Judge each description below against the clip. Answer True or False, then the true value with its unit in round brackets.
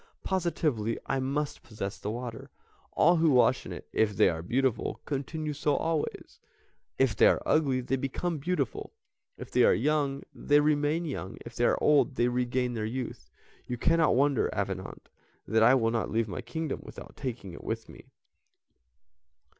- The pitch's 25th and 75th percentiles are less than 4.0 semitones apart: False (4.5 semitones)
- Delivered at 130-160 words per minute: False (170 wpm)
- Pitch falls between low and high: False (130 Hz)